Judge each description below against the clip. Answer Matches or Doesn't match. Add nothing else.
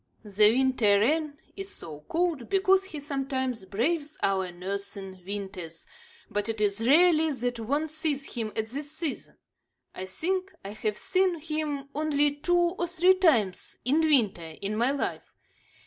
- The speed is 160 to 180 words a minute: Doesn't match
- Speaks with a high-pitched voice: Matches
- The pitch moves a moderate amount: Doesn't match